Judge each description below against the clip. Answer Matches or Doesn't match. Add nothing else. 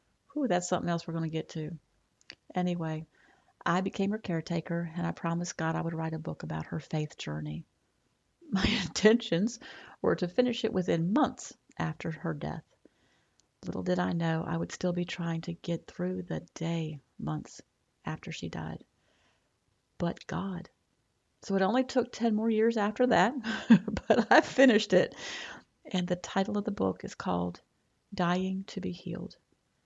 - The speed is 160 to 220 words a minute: Matches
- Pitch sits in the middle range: Matches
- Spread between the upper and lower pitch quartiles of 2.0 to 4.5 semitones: Matches